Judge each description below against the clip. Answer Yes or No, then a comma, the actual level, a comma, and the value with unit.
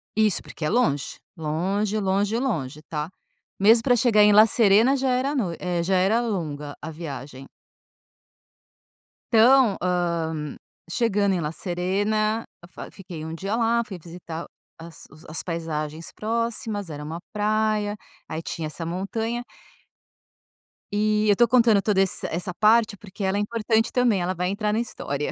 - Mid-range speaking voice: No, high, 200 Hz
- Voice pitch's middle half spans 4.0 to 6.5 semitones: Yes, average, 4.8 semitones